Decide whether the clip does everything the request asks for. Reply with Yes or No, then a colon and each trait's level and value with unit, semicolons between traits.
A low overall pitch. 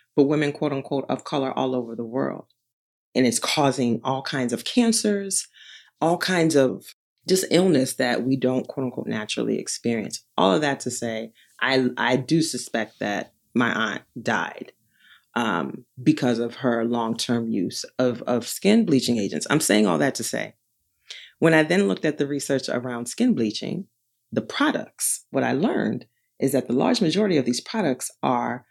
Yes: low, 130 Hz